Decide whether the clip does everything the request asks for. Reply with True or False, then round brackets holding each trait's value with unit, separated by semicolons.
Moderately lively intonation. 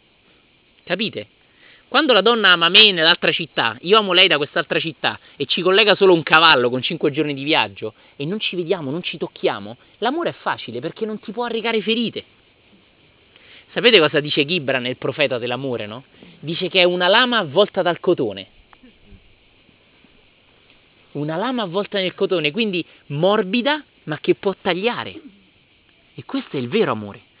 False (6.2 semitones)